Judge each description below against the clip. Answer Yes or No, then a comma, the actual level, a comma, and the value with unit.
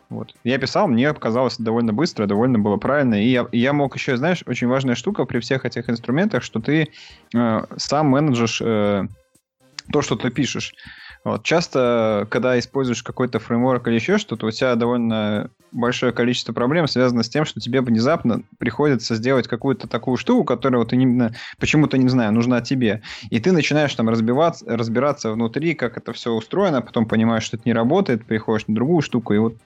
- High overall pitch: No, low, 120 Hz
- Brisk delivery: Yes, fast, 185 wpm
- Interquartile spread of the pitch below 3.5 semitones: Yes, average, 2.8 semitones